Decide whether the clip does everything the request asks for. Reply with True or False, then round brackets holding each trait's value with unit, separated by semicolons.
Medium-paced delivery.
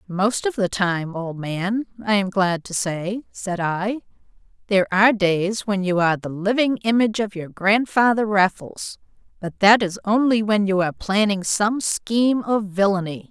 True (170 wpm)